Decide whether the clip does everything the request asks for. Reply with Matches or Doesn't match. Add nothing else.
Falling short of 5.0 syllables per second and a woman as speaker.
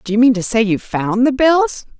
Doesn't match